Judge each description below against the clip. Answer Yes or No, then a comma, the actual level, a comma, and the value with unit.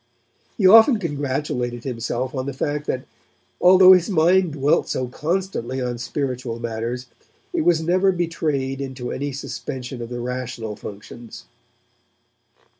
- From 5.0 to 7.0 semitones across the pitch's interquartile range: Yes, wide, 5.4 semitones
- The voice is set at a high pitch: No, low, 135 Hz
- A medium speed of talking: No, slow, 130 wpm